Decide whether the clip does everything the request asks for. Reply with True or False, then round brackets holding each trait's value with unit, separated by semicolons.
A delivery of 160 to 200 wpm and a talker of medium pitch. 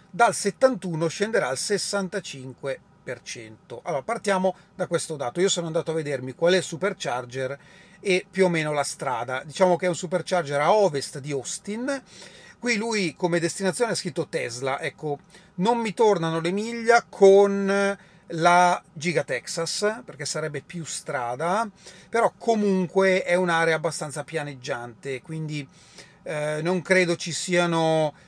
False (140 wpm; 175 Hz)